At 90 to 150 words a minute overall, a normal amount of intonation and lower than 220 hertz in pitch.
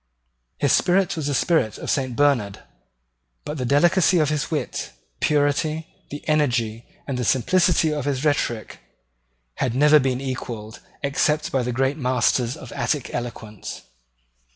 Yes: average, 145 wpm; average, 3.7 semitones; medium, 140 Hz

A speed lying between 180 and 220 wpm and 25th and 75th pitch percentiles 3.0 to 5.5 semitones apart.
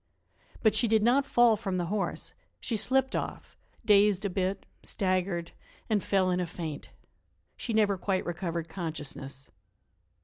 No: average, 145 wpm; average, 3.8 semitones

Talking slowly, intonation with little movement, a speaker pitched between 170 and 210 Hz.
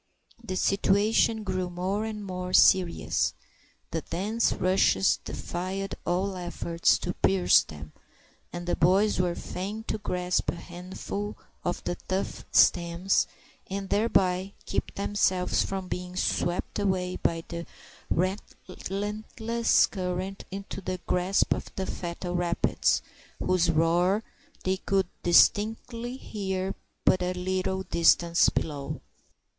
Yes: slow, 120 wpm; narrow, 2.0 semitones; medium, 185 Hz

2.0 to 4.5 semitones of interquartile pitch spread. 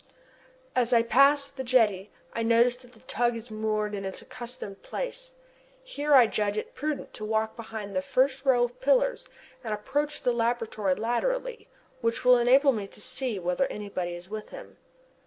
Yes: average, 3.9 semitones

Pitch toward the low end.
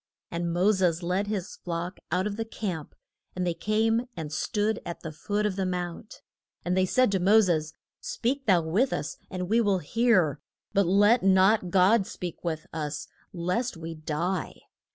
No: medium, 185 Hz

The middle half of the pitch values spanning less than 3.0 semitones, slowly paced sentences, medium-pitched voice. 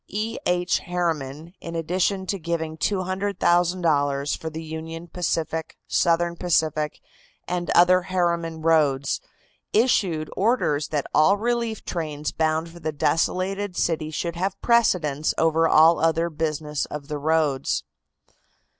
Yes: narrow, 2.5 semitones; slow, 125 wpm; medium, 165 Hz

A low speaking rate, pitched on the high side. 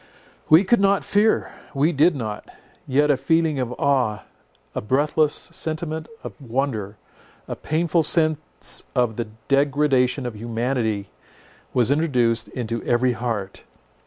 No: slow, 125 wpm; low, 135 Hz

